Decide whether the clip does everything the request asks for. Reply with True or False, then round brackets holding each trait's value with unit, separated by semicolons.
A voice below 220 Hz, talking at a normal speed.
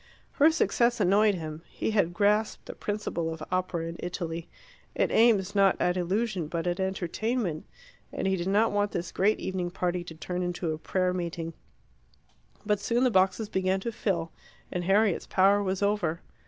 True (190 Hz; 175 wpm)